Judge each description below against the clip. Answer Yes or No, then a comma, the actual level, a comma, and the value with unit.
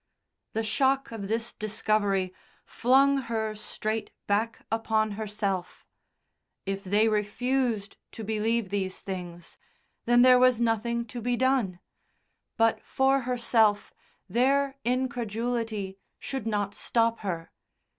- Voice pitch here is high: Yes, high, 225 Hz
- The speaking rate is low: Yes, slow, 115 wpm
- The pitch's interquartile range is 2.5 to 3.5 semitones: Yes, average, 2.9 semitones